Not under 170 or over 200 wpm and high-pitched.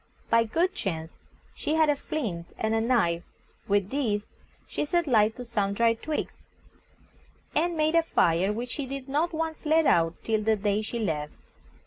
Yes: average, 175 wpm; high, 230 Hz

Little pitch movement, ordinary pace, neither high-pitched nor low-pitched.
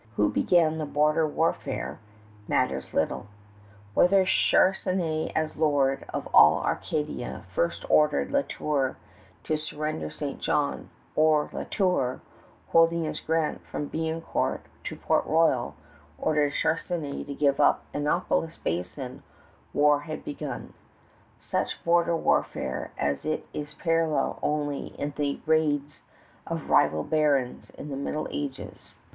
No: narrow, 2.2 semitones; slow, 125 wpm; medium, 150 Hz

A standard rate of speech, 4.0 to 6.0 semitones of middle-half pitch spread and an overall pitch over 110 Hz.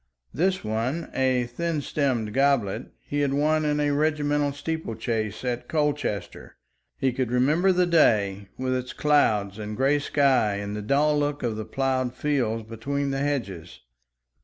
Yes: average, 160 wpm; average, 4.7 semitones; low, 135 Hz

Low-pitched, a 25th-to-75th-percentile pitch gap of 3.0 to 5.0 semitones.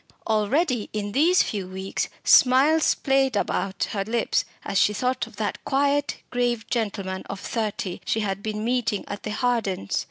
No: high, 220 Hz; average, 4.0 semitones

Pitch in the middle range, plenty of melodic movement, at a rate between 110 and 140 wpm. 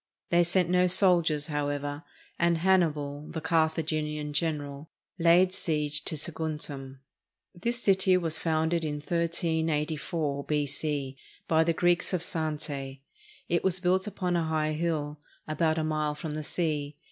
No: medium, 160 Hz; narrow, 2.4 semitones; slow, 135 wpm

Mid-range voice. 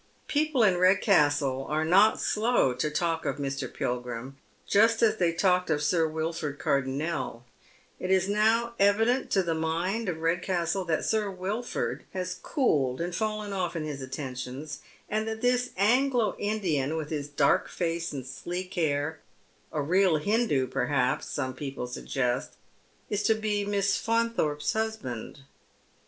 Yes: medium, 170 Hz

